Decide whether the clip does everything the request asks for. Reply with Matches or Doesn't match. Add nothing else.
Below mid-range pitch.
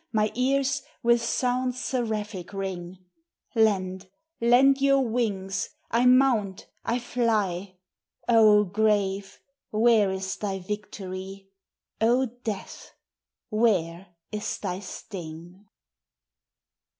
Doesn't match